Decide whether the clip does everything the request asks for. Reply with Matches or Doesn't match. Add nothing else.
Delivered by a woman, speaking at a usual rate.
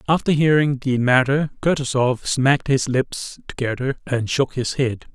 Doesn't match